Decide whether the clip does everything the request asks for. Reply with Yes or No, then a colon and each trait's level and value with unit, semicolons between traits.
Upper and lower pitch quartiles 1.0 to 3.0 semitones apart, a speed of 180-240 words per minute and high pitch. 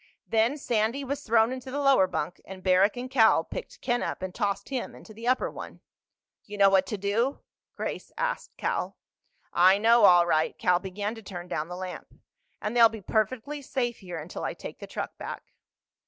No: average, 4.8 semitones; average, 200 wpm; high, 215 Hz